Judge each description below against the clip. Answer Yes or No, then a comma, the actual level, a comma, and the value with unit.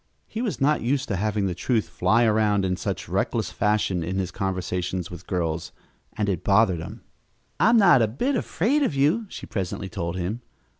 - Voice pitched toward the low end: Yes, low, 105 Hz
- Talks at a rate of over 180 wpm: Yes, average, 190 wpm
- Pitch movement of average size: No, wide, 6.8 semitones